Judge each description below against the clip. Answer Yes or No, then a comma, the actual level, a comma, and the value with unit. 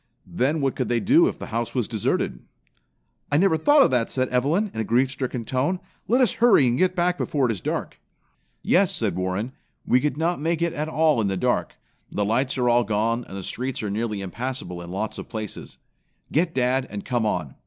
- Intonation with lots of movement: Yes, wide, 6.1 semitones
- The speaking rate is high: Yes, fast, 220 wpm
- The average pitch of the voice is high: No, low, 125 Hz